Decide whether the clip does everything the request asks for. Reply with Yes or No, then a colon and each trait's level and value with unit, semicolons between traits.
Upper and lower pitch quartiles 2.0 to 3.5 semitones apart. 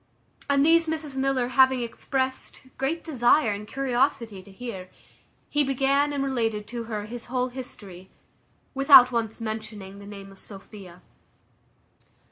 No: average, 4.4 semitones